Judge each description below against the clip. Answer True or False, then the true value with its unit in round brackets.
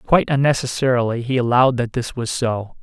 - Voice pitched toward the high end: False (125 Hz)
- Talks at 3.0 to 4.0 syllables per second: False (6.0 syllables/s)